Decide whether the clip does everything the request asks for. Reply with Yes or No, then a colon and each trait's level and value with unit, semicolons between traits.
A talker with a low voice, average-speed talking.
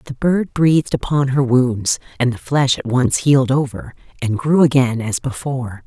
Yes: low, 130 Hz; average, 185 wpm